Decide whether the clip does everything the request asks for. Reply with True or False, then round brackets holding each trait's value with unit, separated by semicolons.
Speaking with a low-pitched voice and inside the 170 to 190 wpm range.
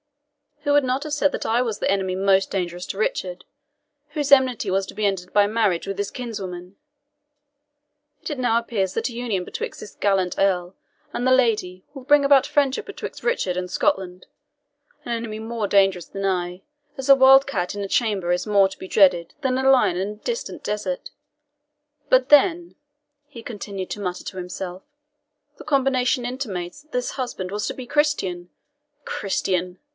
False (210 Hz; 180 wpm)